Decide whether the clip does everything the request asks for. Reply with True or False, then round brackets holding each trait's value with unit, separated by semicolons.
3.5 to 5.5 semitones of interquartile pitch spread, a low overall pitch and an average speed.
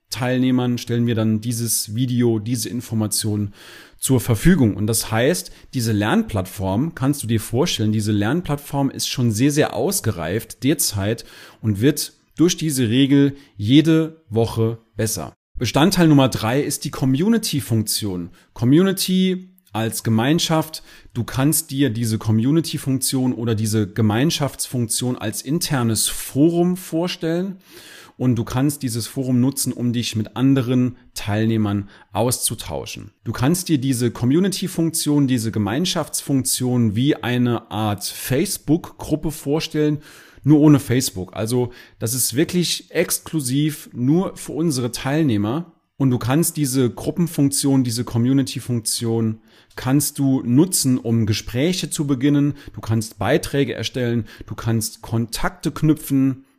False (5.0 semitones; 125 Hz; 120 wpm)